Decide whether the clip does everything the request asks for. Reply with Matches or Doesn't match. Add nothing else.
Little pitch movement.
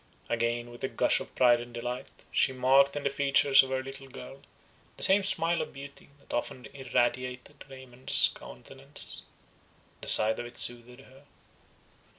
Matches